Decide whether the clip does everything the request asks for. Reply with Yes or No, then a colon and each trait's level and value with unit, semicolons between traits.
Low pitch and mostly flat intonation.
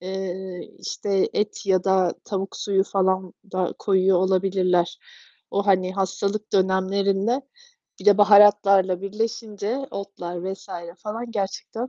No: high, 195 Hz; narrow, 1.5 semitones